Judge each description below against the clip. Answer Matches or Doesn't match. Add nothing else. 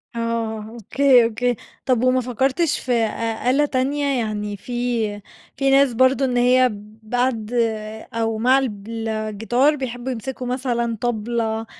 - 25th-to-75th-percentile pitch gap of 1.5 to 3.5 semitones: Matches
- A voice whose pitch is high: Matches